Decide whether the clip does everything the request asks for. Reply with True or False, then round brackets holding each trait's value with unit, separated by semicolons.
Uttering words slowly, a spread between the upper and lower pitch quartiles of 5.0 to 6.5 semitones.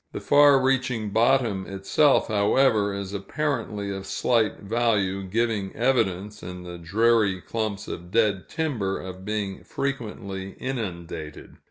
False (125 wpm; 3.6 semitones)